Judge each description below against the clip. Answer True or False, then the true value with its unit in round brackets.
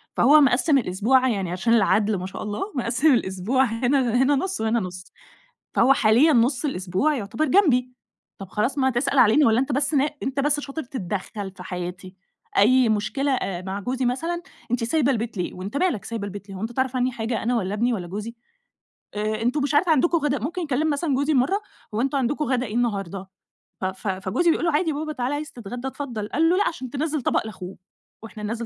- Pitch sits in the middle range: False (245 Hz)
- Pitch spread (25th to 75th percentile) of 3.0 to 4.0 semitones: False (5.3 semitones)